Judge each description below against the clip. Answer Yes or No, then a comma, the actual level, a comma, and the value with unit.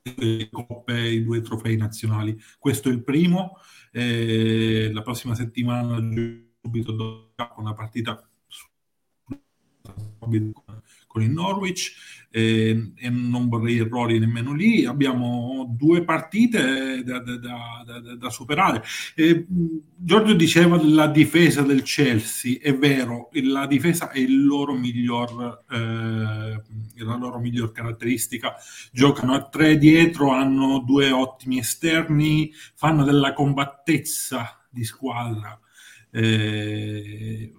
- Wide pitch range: No, average, 3.8 semitones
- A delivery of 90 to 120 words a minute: Yes, slow, 115 wpm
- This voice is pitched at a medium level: No, low, 120 Hz